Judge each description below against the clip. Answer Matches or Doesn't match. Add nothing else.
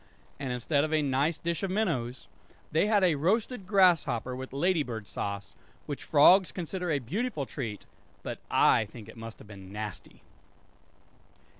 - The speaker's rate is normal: Matches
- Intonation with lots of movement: Matches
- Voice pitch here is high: Doesn't match